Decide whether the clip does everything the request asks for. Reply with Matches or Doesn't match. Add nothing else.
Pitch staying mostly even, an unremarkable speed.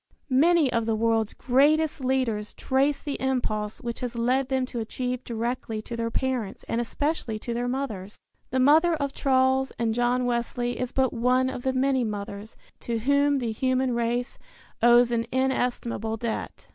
Matches